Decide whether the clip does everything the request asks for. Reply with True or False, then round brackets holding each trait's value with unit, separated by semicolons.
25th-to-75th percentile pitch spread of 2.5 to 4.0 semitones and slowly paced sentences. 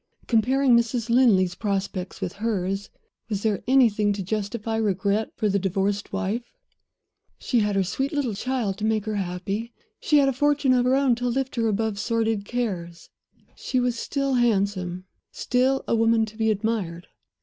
False (3.7 semitones; 170 wpm)